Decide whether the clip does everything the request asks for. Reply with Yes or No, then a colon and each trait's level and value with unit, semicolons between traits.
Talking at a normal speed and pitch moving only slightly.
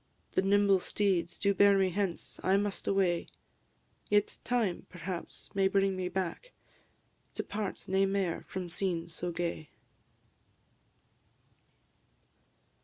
No: slow, 115 wpm; narrow, 2.1 semitones